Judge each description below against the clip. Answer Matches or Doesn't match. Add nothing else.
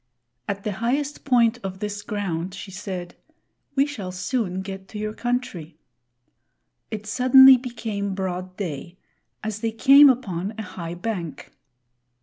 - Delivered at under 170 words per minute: Matches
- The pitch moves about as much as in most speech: Matches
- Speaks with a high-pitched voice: Matches